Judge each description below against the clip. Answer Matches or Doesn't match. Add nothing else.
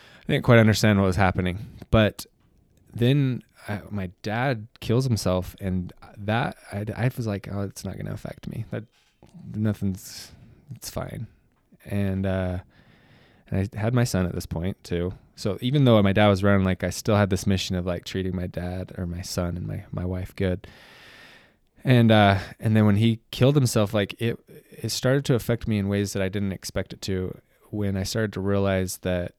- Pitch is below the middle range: Matches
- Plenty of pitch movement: Doesn't match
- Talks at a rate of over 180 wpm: Matches